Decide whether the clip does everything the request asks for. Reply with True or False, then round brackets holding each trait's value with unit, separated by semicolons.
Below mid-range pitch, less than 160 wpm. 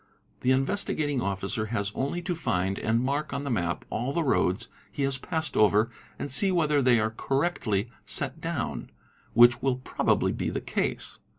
False (130 Hz; 175 wpm)